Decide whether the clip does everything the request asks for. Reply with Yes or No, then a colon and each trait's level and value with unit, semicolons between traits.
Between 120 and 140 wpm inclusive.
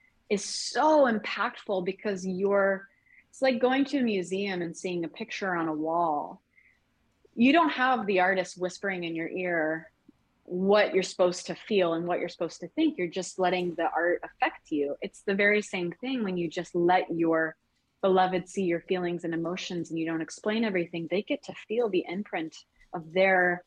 No: average, 190 wpm